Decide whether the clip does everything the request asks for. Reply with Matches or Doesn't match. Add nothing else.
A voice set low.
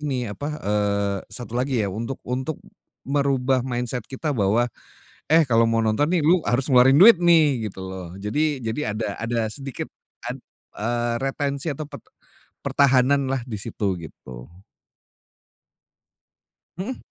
Matches